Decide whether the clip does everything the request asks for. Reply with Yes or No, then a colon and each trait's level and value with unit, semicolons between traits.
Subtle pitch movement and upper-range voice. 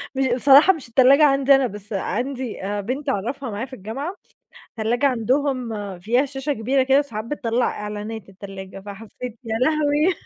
No: average, 4.0 semitones; very high, 250 Hz